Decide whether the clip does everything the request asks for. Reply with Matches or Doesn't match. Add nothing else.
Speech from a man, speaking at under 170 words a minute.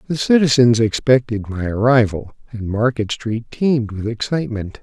Matches